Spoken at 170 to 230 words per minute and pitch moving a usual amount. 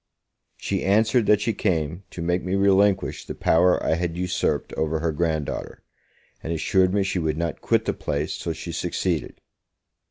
Yes: average, 180 wpm; average, 3.2 semitones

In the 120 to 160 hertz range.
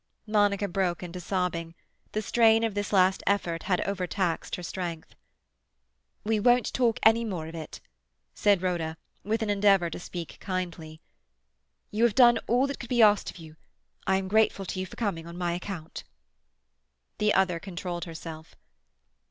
No: high, 190 Hz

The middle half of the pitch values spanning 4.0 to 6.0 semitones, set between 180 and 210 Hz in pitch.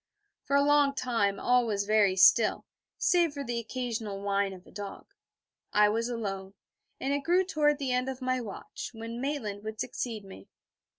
No: average, 5.2 semitones; high, 235 Hz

